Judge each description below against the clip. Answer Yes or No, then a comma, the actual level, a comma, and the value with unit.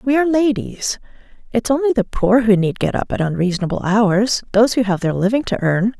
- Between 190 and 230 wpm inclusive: Yes, average, 200 wpm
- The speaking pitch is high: Yes, high, 220 Hz